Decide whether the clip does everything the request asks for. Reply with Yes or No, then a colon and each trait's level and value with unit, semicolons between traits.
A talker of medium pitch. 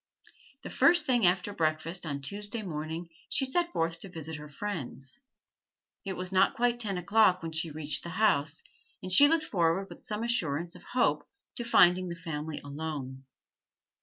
Yes: medium, 175 Hz